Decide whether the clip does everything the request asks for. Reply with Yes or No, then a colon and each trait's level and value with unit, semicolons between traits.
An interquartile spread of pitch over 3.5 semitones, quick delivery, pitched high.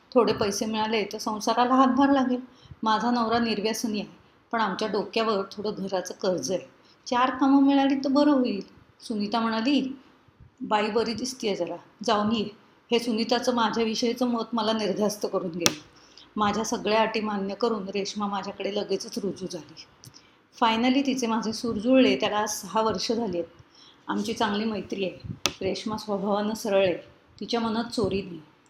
No: average, 2.8 semitones; fast, 155 wpm; high, 220 Hz